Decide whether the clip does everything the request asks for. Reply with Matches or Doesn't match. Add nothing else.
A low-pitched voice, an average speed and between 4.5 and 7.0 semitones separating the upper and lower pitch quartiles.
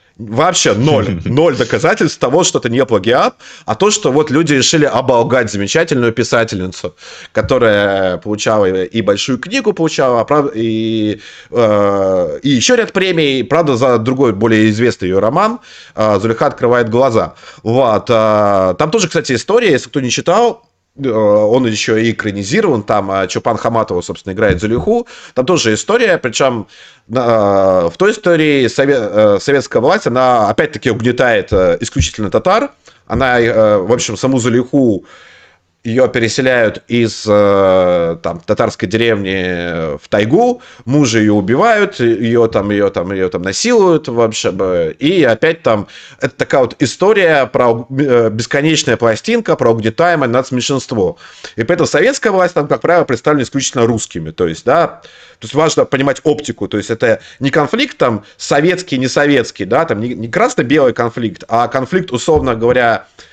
Matches